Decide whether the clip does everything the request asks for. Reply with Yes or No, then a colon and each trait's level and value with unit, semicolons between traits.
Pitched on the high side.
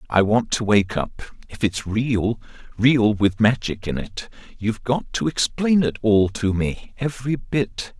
No: low, 110 Hz